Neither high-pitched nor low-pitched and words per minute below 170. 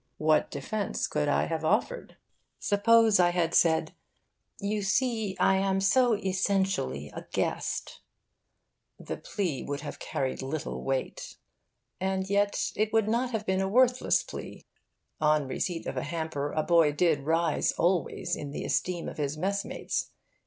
Yes: medium, 180 Hz; average, 150 wpm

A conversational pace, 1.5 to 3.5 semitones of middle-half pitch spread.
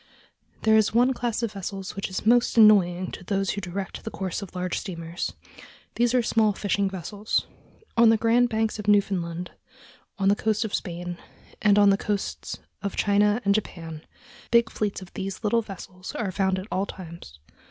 Yes: average, 185 wpm; average, 2.8 semitones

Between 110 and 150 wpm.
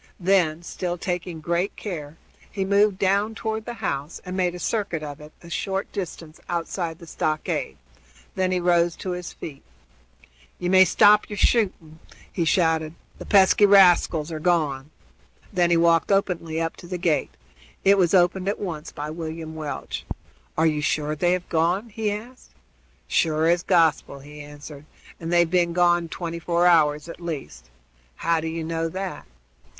No: average, 165 wpm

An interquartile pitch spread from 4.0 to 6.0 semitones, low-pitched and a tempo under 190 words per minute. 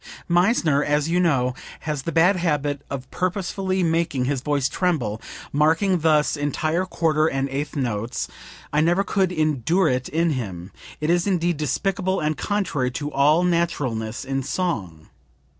No: average, 4.3 semitones; medium, 155 Hz; average, 150 wpm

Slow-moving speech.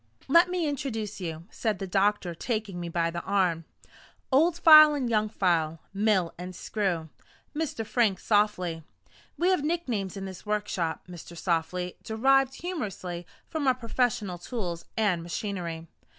No: average, 145 wpm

